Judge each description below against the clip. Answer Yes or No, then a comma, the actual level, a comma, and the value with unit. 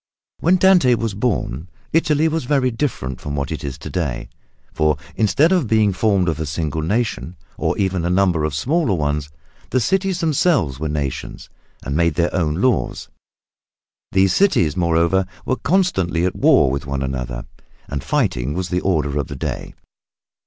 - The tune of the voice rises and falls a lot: Yes, wide, 9.0 semitones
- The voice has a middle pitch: No, very low, 90 Hz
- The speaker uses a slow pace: No, average, 175 wpm